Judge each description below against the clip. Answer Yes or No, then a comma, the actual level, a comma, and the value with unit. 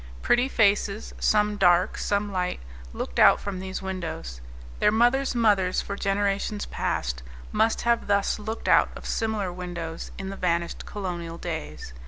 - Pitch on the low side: No, high, 195 Hz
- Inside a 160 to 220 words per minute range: No, average, 150 wpm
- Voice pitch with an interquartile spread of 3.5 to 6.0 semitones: No, average, 3.1 semitones